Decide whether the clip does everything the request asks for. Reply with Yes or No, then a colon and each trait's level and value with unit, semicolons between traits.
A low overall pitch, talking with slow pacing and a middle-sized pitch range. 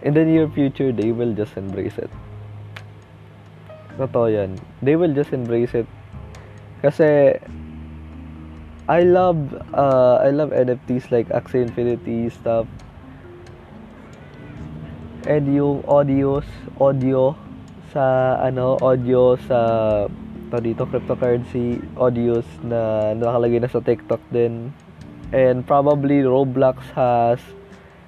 Yes: low, 120 Hz; slow, 105 wpm; average, 3.8 semitones